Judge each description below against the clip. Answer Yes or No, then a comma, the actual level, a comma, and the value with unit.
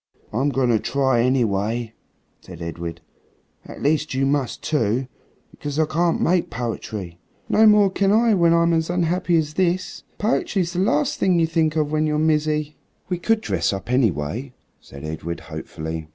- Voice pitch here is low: No, medium, 145 Hz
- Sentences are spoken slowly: No, average, 165 wpm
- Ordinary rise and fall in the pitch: No, wide, 7.1 semitones